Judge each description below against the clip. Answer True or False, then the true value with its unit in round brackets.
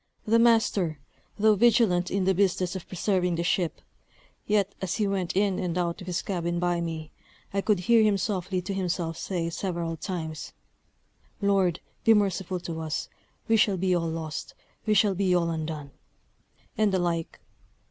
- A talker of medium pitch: True (180 Hz)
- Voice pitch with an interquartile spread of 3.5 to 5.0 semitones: False (2.8 semitones)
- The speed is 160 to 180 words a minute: True (170 wpm)